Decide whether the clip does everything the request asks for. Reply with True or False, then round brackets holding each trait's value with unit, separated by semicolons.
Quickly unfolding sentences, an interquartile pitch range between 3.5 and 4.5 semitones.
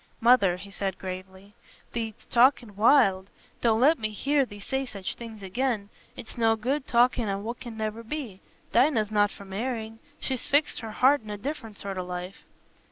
False (180 wpm; 3.9 semitones)